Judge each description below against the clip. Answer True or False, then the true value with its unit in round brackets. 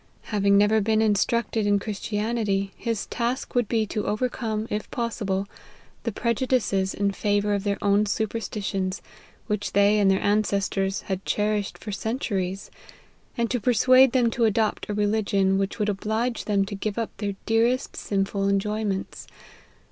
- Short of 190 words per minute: True (155 wpm)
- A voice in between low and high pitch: False (210 Hz)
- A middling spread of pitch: False (2.2 semitones)